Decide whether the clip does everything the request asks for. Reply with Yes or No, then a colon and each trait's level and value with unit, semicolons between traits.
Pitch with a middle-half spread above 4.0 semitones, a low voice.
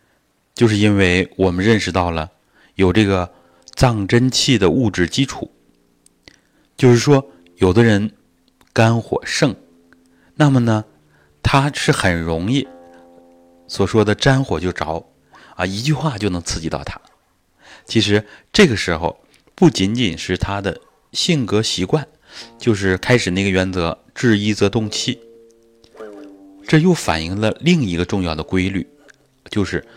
Yes: average, 5.2 semitones; low, 100 Hz